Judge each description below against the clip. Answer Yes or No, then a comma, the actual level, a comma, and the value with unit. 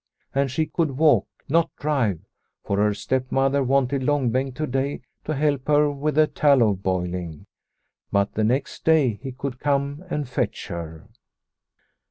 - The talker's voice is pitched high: No, low, 135 Hz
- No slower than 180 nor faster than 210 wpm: No, average, 155 wpm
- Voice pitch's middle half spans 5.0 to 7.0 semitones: No, average, 4.6 semitones